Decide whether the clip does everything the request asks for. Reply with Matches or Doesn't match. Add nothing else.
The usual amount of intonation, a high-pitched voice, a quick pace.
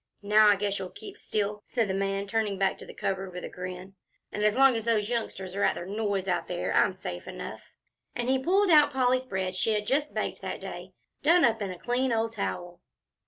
Matches